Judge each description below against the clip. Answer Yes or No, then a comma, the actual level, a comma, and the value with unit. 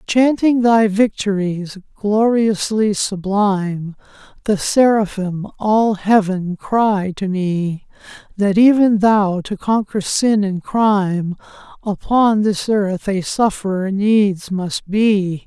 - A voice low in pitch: No, high, 205 Hz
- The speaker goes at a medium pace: No, slow, 100 wpm